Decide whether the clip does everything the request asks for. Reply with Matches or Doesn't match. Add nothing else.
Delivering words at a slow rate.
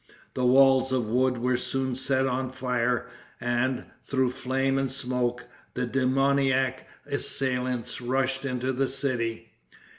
Matches